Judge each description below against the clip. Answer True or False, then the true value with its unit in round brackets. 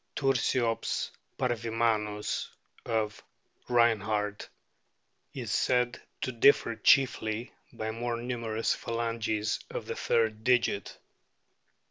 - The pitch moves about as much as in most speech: False (1.8 semitones)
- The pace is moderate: False (85 wpm)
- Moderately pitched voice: False (115 Hz)